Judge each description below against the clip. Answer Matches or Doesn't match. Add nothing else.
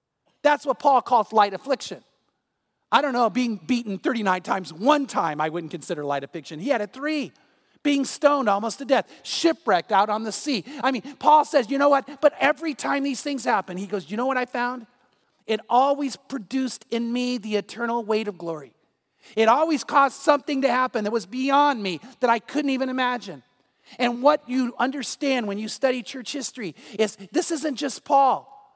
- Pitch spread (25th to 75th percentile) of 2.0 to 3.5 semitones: Doesn't match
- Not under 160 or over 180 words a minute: Doesn't match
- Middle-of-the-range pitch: Doesn't match